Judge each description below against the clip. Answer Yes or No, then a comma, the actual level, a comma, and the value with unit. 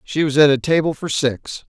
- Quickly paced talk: Yes, fast, 240 wpm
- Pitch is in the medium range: Yes, medium, 145 Hz